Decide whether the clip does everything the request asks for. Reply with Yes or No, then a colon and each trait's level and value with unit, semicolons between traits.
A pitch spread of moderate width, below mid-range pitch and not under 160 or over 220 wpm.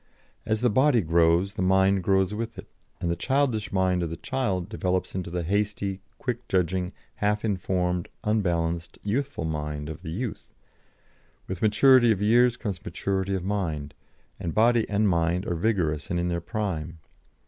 Yes: average, 3.9 semitones; very low, 95 Hz; average, 165 wpm